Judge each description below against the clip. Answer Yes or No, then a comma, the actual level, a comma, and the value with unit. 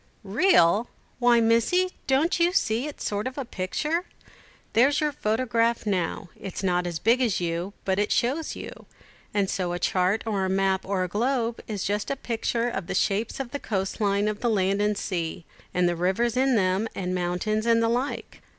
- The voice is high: Yes, high, 215 Hz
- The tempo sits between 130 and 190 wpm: No, fast, 205 wpm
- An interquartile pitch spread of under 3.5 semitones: No, average, 4.2 semitones